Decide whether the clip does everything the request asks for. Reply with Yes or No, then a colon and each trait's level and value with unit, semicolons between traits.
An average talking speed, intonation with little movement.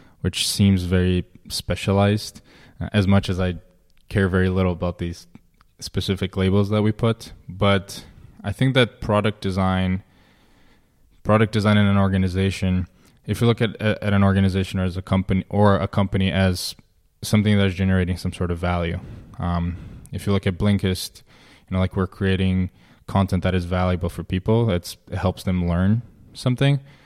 Yes: average, 160 wpm; narrow, 2.2 semitones